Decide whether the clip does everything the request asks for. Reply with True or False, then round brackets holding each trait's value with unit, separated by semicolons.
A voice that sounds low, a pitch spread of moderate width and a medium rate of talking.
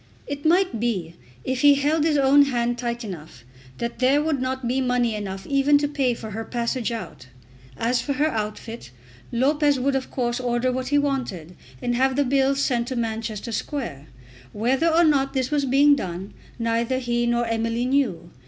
False (250 Hz; 3.3 semitones; 185 wpm)